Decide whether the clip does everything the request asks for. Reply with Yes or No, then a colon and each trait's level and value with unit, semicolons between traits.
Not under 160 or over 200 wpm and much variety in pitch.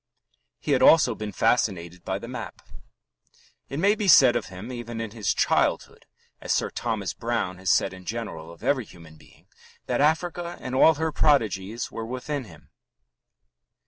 Yes: average, 170 wpm; wide, 6.6 semitones